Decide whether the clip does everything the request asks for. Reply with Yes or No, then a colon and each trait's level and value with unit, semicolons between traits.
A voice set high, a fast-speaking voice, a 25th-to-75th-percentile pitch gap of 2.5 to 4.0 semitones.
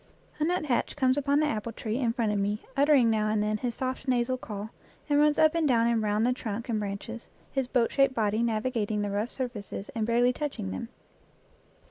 Yes: high, 235 Hz; fast, 210 wpm; average, 3.6 semitones